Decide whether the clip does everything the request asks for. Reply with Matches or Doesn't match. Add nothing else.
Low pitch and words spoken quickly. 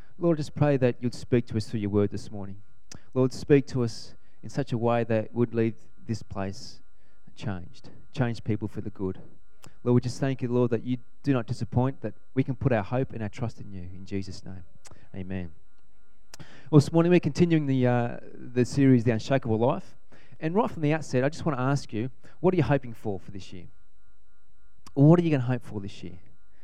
Matches